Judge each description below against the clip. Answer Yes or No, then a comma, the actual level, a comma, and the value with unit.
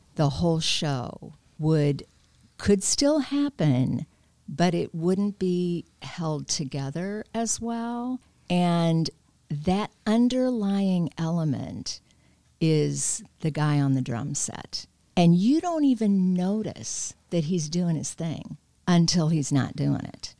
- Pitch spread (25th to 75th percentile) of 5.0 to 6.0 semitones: Yes, wide, 5.6 semitones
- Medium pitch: Yes, medium, 170 Hz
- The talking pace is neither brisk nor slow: No, slow, 120 wpm